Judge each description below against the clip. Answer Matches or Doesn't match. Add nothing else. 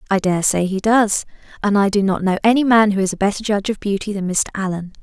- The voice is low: Doesn't match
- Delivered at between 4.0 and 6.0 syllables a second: Doesn't match